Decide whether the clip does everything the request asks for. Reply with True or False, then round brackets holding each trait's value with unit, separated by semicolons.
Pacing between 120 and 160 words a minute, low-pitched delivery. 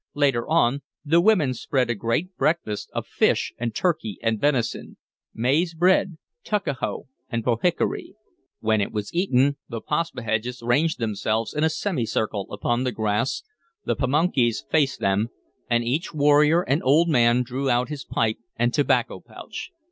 True (150 wpm; 130 Hz)